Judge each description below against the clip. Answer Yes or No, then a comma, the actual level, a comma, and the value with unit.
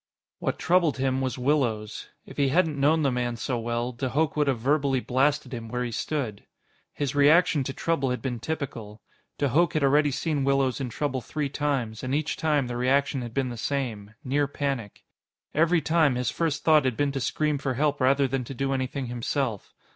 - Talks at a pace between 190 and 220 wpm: Yes, fast, 205 wpm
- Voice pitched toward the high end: No, low, 135 Hz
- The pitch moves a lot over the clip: No, average, 2.9 semitones